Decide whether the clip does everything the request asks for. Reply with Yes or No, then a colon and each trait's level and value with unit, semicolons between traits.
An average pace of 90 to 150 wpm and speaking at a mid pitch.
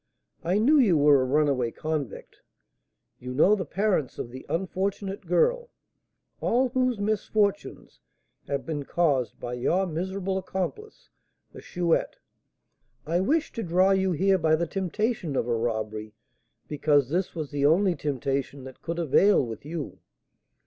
Yes: average, 145 wpm; medium, 170 Hz